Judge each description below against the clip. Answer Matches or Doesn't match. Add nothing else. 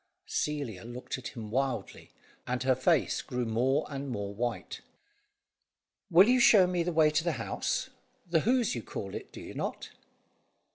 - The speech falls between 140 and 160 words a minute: Doesn't match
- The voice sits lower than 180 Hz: Matches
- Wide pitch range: Matches